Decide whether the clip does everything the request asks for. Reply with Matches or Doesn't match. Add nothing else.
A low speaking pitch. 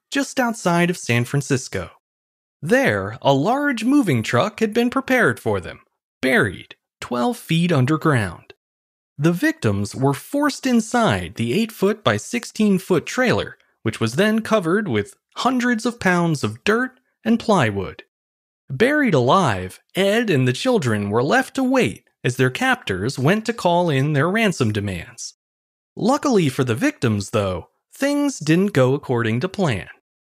Doesn't match